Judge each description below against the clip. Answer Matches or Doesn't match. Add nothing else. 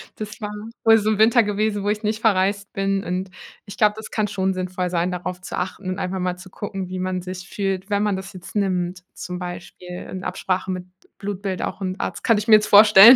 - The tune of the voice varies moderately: Doesn't match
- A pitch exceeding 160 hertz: Matches